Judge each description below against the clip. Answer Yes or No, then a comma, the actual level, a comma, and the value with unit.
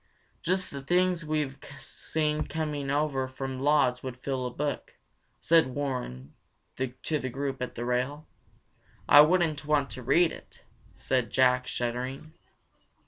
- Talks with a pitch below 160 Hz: Yes, medium, 140 Hz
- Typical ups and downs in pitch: Yes, average, 3.0 semitones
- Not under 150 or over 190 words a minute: No, average, 140 wpm